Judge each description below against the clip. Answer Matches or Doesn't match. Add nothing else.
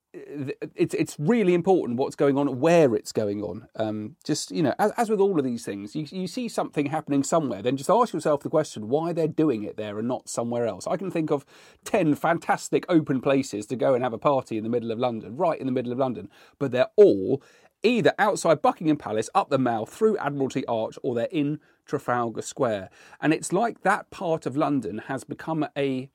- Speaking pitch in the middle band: Matches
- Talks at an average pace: Doesn't match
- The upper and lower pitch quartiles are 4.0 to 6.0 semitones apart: Matches